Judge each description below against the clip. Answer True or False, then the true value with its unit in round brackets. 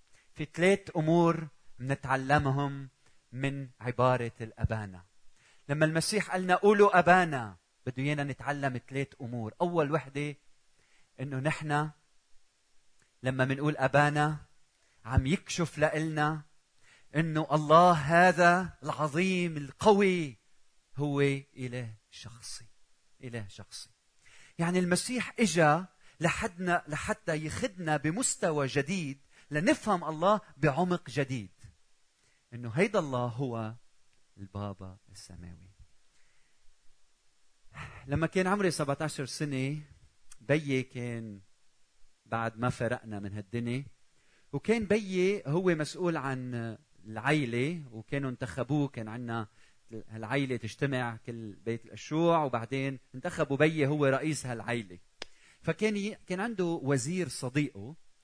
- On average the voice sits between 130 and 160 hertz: True (140 Hz)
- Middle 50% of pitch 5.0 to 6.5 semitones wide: True (5.5 semitones)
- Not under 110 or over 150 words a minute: False (95 wpm)